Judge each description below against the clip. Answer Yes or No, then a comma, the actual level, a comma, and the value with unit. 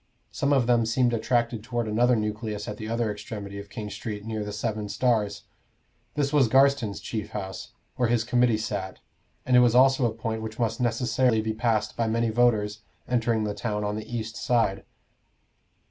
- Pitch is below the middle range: Yes, low, 115 Hz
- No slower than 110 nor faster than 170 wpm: No, average, 185 wpm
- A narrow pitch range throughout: Yes, narrow, 2.2 semitones